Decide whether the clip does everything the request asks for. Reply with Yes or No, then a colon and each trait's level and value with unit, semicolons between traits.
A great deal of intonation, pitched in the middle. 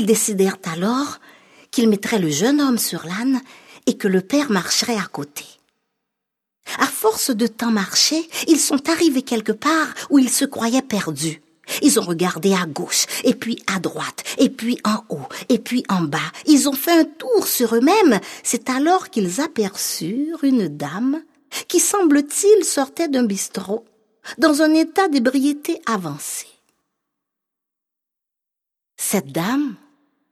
No: wide, 5.7 semitones; high, 245 Hz